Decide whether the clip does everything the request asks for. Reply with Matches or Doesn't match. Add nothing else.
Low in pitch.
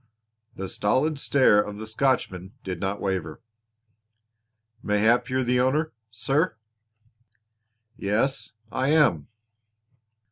Matches